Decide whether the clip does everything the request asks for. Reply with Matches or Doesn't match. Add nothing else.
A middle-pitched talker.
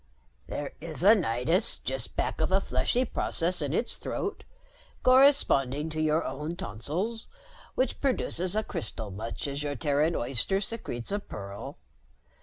Matches